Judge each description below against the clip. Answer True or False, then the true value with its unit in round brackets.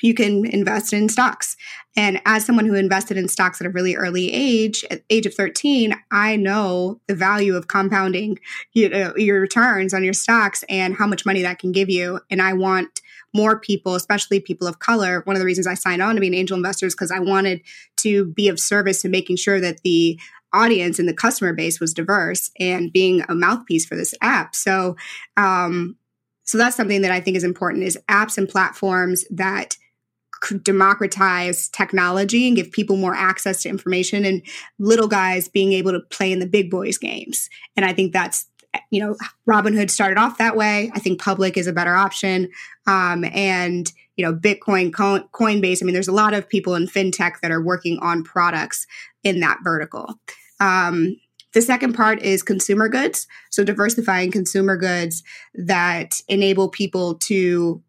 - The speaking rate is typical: True (190 wpm)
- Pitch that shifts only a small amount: True (2.1 semitones)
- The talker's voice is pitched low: False (195 Hz)